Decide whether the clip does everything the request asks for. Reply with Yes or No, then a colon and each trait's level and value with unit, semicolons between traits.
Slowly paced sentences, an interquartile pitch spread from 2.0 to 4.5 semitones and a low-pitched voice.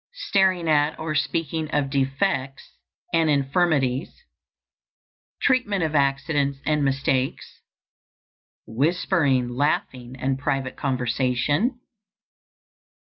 No: slow, 85 wpm; average, 3.4 semitones; medium, 145 Hz